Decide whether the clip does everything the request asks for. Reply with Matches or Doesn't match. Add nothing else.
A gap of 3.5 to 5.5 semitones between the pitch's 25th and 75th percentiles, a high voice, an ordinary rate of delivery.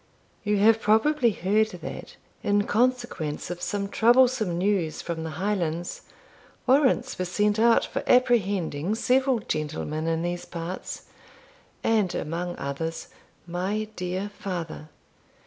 Doesn't match